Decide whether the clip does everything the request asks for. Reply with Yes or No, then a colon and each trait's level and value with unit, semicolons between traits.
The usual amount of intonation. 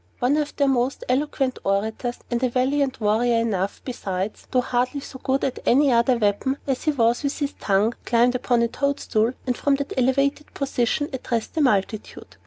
Yes: average, 3.1 semitones